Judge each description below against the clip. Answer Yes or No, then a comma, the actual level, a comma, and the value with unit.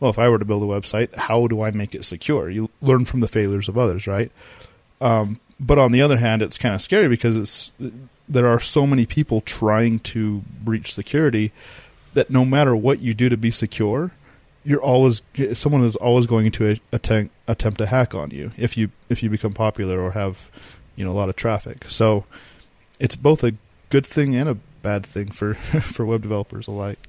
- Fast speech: Yes, fast, 210 wpm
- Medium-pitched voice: No, low, 115 Hz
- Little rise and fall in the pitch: No, average, 3.1 semitones